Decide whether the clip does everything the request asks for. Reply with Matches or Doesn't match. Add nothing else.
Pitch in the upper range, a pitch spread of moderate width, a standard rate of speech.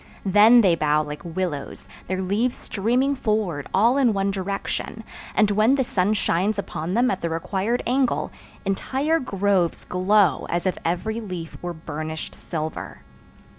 Matches